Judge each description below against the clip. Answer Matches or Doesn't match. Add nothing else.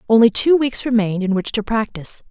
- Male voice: Doesn't match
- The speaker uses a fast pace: Matches